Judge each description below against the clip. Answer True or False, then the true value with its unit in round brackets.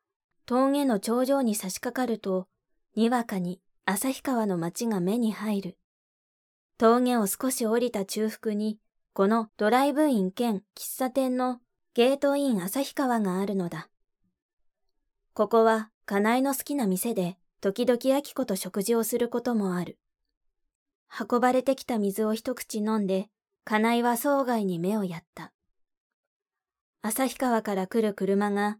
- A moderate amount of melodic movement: True (4.1 semitones)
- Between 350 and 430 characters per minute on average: False (250 characters per minute)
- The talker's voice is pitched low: False (225 Hz)